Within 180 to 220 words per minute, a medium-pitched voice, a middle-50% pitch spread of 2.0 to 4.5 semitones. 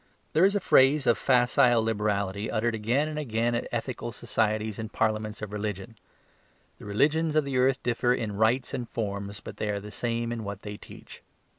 No: average, 190 wpm; low, 115 Hz; average, 3.1 semitones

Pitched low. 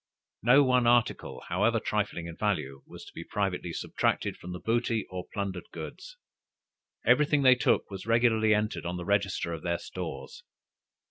Yes: low, 105 Hz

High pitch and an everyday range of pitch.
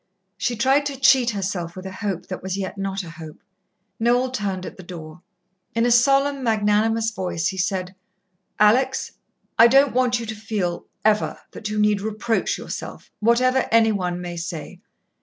Yes: high, 210 Hz; average, 4.2 semitones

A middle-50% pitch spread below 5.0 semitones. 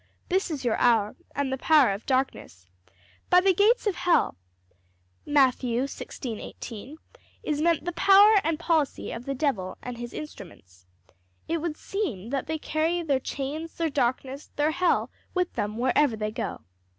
No: wide, 5.5 semitones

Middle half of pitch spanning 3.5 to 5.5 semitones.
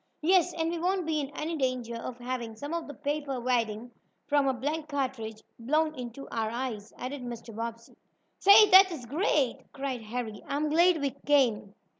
Yes: average, 4.7 semitones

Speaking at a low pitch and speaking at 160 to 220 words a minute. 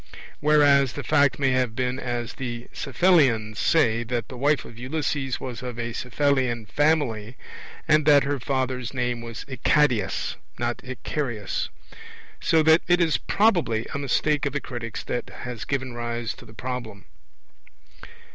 No: low, 130 Hz; average, 150 wpm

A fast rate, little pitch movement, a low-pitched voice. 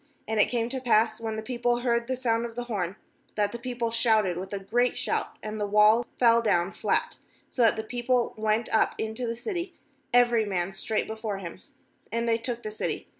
No: fast, 215 wpm; narrow, 2.1 semitones; high, 230 Hz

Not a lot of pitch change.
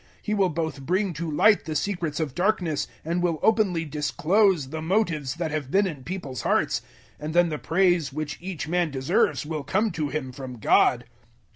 No: average, 3.7 semitones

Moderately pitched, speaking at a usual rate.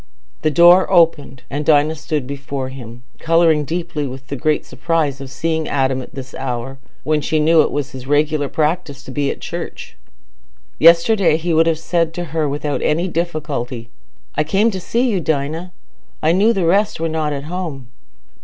Yes: medium, 155 Hz; average, 180 wpm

